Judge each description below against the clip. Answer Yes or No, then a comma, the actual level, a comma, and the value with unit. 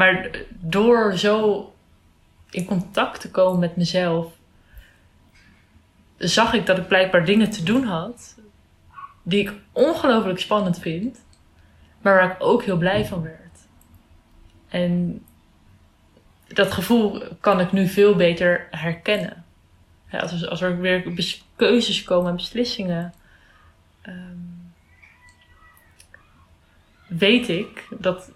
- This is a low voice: No, medium, 175 Hz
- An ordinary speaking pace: No, slow, 105 wpm